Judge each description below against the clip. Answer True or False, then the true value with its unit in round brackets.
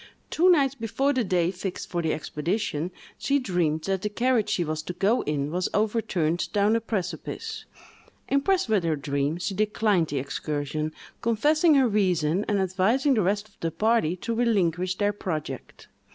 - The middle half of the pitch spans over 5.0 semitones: True (5.6 semitones)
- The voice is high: True (195 Hz)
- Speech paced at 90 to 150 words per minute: False (170 wpm)